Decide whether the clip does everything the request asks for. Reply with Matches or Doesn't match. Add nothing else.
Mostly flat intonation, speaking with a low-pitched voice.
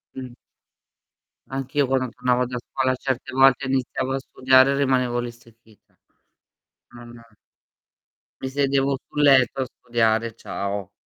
Matches